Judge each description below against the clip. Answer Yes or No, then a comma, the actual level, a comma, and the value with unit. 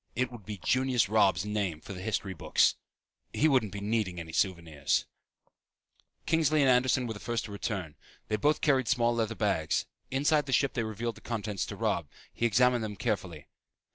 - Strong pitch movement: No, average, 4.4 semitones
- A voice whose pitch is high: No, low, 110 Hz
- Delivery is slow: No, average, 185 wpm